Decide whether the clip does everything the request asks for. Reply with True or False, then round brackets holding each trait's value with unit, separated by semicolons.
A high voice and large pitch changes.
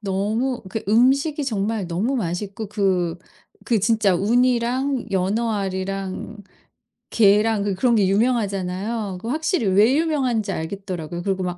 False (210 Hz; 3.8 semitones)